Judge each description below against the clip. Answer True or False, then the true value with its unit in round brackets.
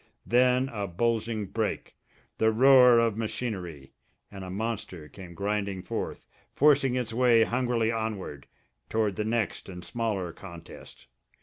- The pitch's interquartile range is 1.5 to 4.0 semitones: True (3.5 semitones)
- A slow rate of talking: True (130 wpm)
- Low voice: True (110 Hz)